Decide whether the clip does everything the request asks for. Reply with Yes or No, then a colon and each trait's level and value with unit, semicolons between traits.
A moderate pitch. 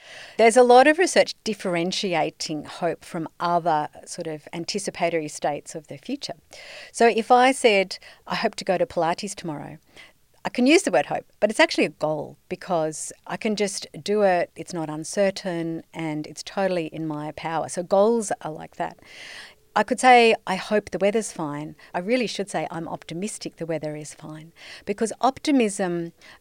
Yes: medium, 180 Hz